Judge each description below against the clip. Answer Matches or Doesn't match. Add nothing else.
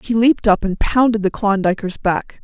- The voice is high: Matches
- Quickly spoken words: Doesn't match